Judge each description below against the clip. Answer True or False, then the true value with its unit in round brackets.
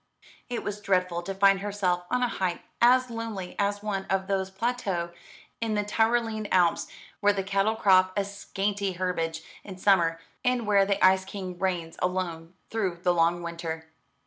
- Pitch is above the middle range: True (195 Hz)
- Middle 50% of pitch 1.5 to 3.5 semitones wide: True (2.5 semitones)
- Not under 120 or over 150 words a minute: False (170 wpm)